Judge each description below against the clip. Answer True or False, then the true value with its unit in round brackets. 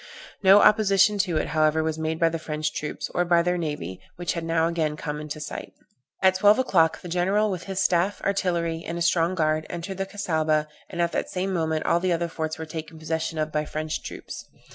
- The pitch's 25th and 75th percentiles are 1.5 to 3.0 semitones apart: True (2.7 semitones)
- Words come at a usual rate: False (220 wpm)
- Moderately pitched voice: True (165 Hz)